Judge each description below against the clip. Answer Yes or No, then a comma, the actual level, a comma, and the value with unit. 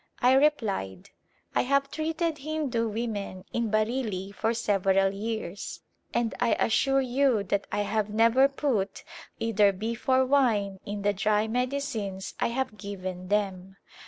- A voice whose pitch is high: Yes, high, 220 Hz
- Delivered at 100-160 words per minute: Yes, average, 145 wpm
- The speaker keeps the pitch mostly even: No, average, 4.5 semitones